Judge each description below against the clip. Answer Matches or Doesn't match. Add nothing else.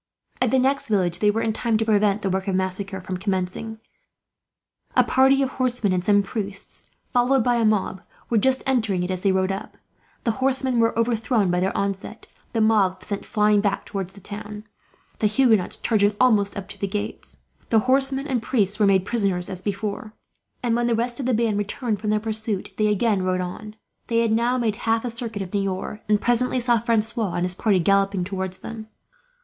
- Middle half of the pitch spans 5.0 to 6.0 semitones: Doesn't match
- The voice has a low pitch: Doesn't match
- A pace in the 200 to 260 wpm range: Matches